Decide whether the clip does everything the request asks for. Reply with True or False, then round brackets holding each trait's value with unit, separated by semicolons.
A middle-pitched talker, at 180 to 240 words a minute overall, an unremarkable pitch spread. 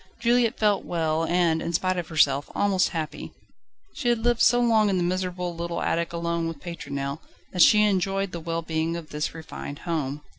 True (170 Hz; 190 wpm; 3.3 semitones)